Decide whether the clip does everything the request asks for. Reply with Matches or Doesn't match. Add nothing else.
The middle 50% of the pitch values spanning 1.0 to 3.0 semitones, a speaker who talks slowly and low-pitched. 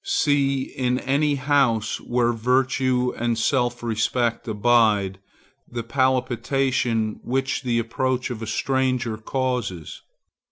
Matches